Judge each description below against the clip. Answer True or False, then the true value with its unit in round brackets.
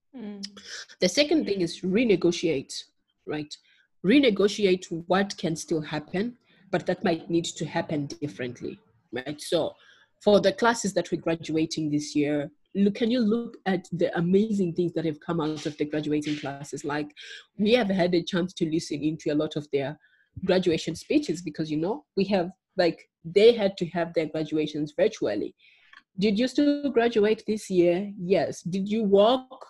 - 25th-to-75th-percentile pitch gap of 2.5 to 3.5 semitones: False (4.2 semitones)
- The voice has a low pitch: False (175 Hz)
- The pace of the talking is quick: False (165 wpm)